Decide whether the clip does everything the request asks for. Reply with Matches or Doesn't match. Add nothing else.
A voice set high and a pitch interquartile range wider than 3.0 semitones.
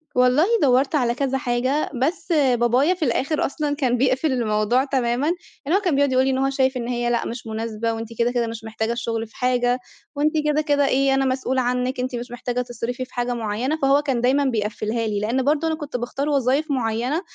Doesn't match